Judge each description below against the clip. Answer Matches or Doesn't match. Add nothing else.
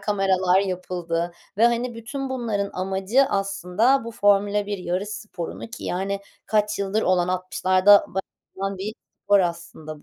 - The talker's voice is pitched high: Matches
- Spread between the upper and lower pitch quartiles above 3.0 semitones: Doesn't match